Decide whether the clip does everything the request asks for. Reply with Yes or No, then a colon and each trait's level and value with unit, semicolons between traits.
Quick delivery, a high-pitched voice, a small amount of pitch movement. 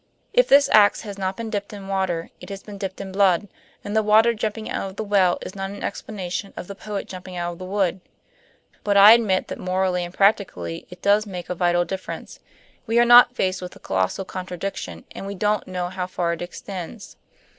Yes: fast, 220 wpm; high, 195 Hz; narrow, 2.3 semitones